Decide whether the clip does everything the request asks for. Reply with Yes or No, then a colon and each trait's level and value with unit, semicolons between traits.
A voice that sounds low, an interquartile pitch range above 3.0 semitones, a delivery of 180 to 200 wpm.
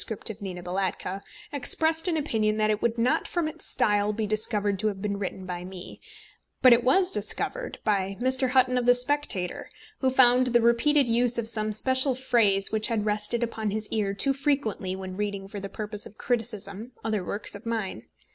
No: high, 220 Hz; average, 3.8 semitones; average, 195 wpm